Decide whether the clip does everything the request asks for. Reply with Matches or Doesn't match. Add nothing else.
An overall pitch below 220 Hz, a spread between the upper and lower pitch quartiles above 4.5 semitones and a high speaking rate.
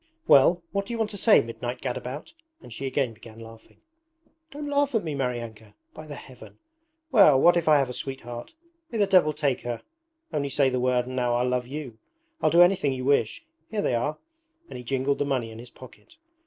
Matches